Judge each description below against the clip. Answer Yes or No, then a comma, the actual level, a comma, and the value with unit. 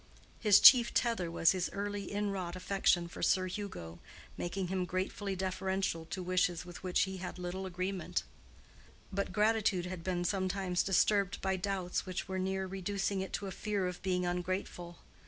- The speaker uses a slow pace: No, average, 165 wpm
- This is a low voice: No, medium, 185 Hz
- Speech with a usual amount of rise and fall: No, narrow, 1.7 semitones